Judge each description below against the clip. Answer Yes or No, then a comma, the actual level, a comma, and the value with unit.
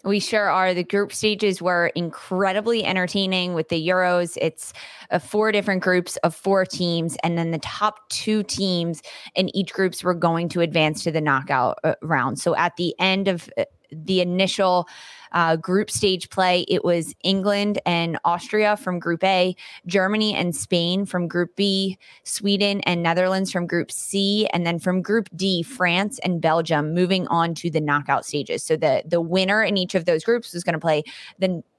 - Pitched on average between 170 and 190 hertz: Yes, medium, 185 Hz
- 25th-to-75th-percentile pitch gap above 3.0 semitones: No, narrow, 2.5 semitones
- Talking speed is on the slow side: No, average, 180 wpm